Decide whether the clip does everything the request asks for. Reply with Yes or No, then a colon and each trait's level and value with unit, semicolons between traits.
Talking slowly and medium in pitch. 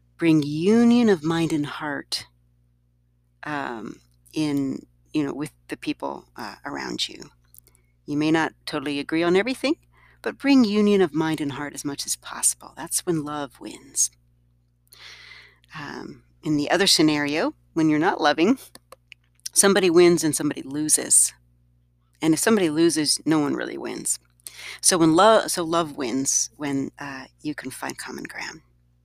No: average, 150 wpm; medium, 150 Hz